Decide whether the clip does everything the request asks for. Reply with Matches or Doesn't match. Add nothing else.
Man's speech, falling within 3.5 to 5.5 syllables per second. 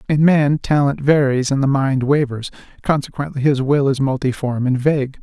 Matches